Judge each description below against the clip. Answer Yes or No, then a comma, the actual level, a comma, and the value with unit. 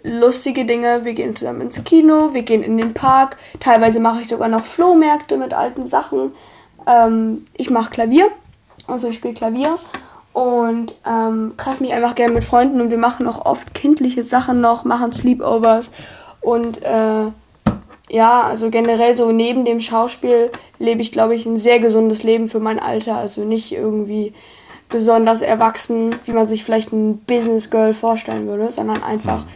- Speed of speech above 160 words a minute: Yes, average, 170 wpm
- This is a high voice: Yes, high, 230 Hz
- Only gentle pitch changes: Yes, narrow, 1.7 semitones